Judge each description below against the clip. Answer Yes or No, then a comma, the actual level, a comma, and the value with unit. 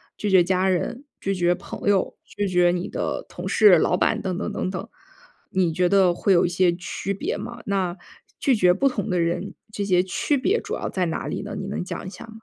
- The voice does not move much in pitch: Yes, narrow, 2.3 semitones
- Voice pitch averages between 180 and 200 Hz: Yes, high, 190 Hz